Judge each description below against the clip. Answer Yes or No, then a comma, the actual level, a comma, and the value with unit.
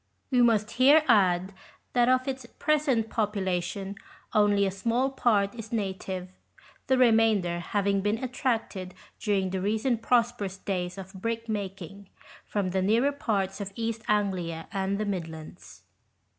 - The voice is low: No, high, 205 Hz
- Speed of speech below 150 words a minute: Yes, average, 140 wpm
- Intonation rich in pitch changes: No, average, 3.3 semitones